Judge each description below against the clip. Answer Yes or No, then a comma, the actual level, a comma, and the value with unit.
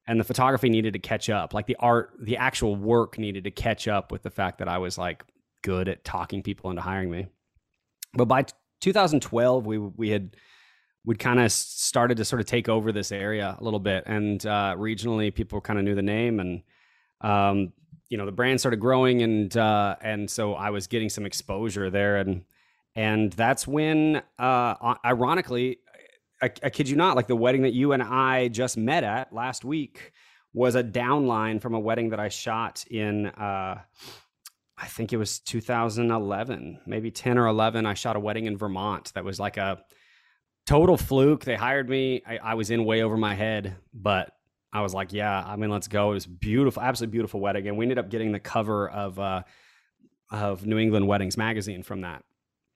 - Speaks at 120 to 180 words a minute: No, average, 200 wpm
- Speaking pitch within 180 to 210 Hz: No, low, 110 Hz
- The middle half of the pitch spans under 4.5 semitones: Yes, average, 3.3 semitones